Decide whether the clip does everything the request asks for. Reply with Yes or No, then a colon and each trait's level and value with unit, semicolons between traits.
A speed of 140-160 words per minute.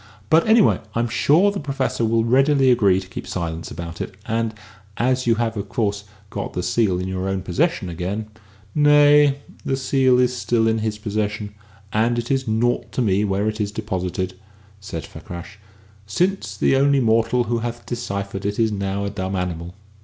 No: average, 185 wpm